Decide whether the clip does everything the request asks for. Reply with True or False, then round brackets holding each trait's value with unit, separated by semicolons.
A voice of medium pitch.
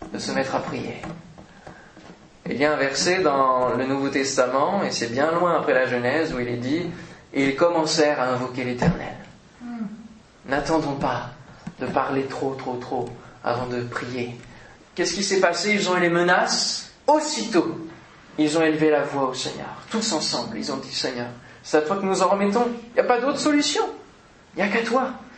True (155 Hz)